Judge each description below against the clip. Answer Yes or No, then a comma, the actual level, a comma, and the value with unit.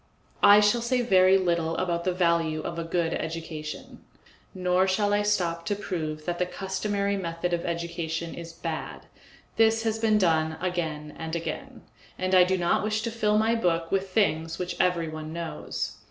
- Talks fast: No, average, 175 wpm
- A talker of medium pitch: Yes, medium, 180 Hz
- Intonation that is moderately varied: Yes, average, 3.5 semitones